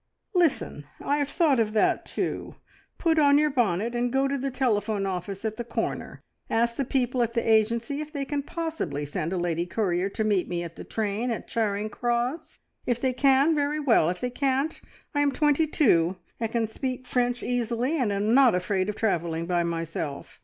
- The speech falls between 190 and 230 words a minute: Yes, average, 200 wpm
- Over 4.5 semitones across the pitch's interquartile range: Yes, wide, 5.5 semitones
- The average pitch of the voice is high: Yes, high, 235 Hz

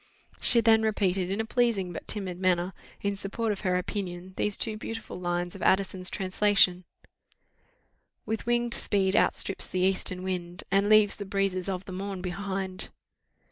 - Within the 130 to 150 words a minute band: No, average, 160 wpm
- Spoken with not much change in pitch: Yes, narrow, 2.2 semitones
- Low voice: No, high, 195 Hz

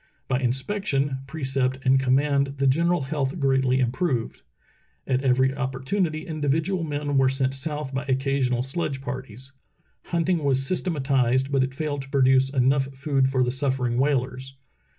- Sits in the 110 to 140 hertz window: Yes, low, 135 Hz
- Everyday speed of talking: Yes, average, 150 wpm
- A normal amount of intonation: No, narrow, 1.8 semitones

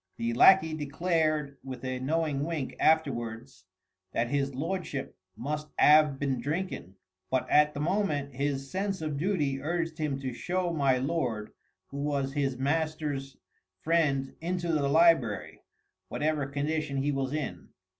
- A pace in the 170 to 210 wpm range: No, average, 140 wpm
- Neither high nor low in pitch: Yes, medium, 145 Hz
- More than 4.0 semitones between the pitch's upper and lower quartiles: No, average, 2.9 semitones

